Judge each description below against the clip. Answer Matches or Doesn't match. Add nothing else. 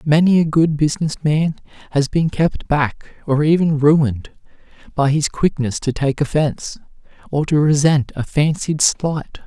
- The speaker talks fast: Doesn't match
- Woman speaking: Doesn't match